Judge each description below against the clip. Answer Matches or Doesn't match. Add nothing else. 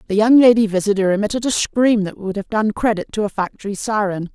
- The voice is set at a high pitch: Matches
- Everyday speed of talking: Doesn't match